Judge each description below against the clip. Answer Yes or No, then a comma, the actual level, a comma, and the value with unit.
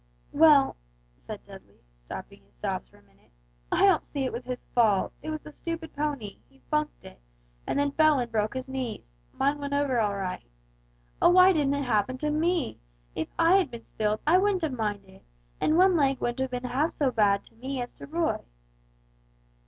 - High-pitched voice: Yes, very high, 270 Hz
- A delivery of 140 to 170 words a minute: No, average, 200 wpm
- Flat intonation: No, wide, 5.6 semitones